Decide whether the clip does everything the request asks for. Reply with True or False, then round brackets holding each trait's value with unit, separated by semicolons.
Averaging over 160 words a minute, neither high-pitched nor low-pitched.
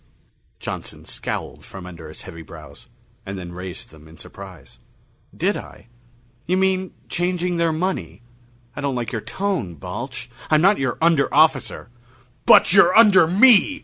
False (150 wpm; 145 Hz)